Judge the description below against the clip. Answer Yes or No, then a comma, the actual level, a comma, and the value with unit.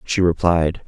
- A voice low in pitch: Yes, very low, 85 Hz